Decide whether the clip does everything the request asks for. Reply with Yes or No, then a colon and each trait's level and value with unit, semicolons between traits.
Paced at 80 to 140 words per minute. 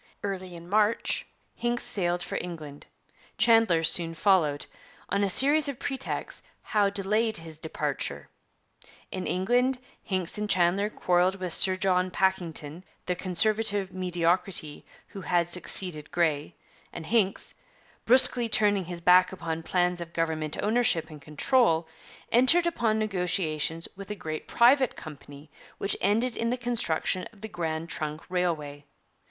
Yes: slow, 135 wpm